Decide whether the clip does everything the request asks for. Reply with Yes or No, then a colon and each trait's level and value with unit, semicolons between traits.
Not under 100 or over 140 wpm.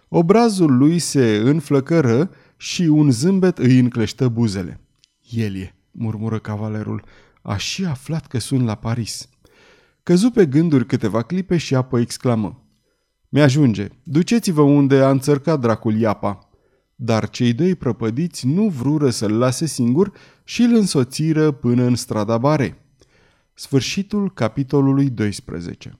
Yes: average, 125 wpm